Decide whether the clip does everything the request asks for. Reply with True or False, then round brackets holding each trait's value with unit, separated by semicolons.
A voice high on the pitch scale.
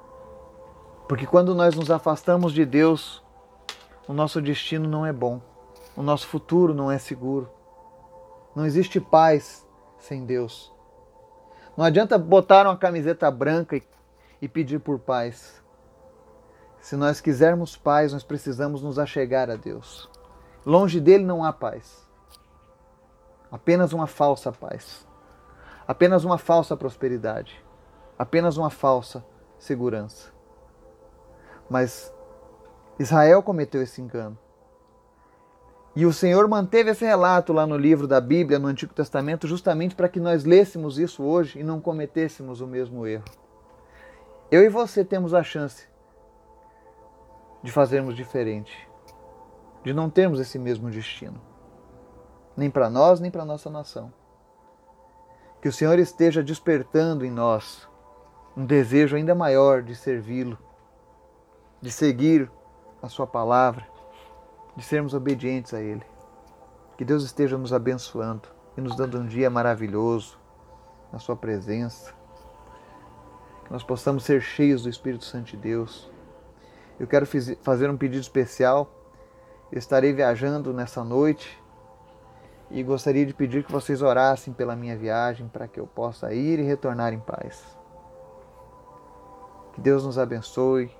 False (140 Hz)